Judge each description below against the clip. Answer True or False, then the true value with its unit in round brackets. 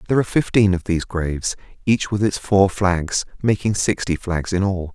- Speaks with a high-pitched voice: False (95 Hz)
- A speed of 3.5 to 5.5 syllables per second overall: True (5.4 syllables/s)